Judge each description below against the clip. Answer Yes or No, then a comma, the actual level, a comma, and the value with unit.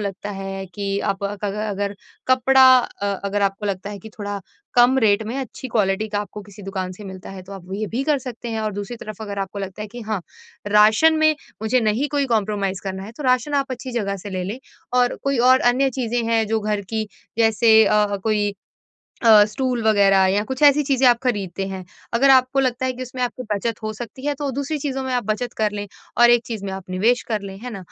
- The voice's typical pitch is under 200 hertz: No, high, 215 Hz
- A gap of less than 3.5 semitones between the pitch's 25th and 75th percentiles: No, average, 3.8 semitones